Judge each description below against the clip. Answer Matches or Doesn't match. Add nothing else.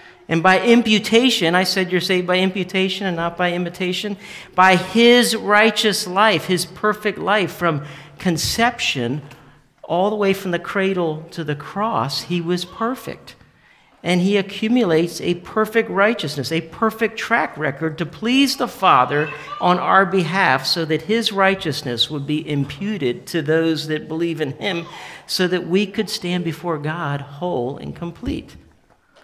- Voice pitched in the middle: Matches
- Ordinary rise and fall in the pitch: Matches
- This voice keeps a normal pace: Matches